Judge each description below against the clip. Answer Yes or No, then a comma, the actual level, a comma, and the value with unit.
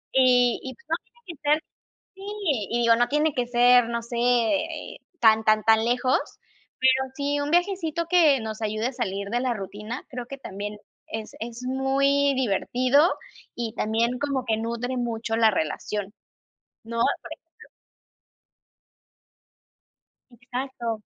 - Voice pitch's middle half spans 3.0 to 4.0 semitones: Yes, average, 3.7 semitones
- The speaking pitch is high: Yes, high, 245 Hz